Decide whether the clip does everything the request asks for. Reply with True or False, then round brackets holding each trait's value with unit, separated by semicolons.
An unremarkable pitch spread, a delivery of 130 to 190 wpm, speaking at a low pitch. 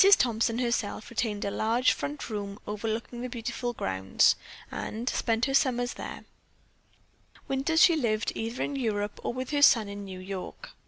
False (3.4 semitones; 160 wpm; 230 Hz)